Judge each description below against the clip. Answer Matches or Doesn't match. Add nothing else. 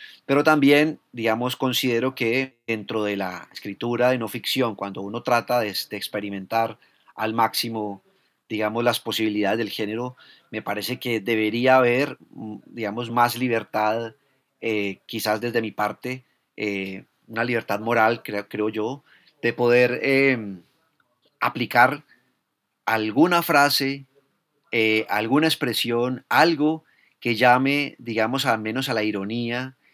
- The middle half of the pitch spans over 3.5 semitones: Doesn't match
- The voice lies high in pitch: Doesn't match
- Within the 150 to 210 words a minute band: Doesn't match